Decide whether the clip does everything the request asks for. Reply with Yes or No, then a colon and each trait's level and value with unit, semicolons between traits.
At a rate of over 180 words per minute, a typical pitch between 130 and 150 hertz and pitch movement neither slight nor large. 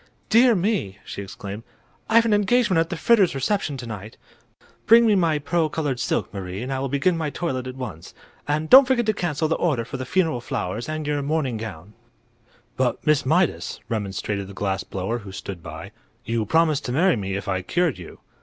No: average, 200 wpm; medium, 140 Hz; wide, 8.5 semitones